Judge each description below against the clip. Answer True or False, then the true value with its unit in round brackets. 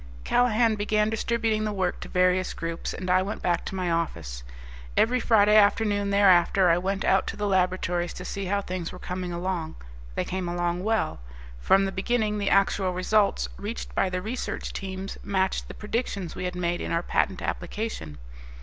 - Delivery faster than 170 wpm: True (185 wpm)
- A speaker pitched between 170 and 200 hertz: True (190 Hz)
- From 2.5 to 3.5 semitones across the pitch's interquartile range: True (2.8 semitones)